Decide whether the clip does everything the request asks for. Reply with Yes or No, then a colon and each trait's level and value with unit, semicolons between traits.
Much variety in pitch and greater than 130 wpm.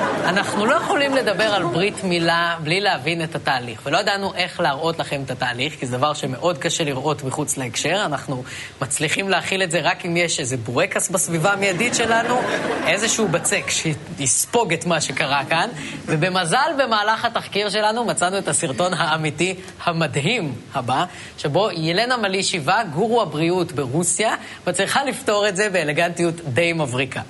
No: average, 5.0 semitones; fast, 150 wpm